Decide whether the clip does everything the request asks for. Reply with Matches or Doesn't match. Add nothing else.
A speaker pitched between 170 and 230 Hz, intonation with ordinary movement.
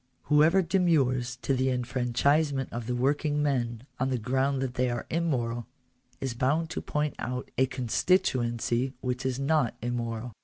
Doesn't match